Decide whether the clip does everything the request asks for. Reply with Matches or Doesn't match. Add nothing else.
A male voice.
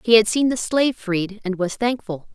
Doesn't match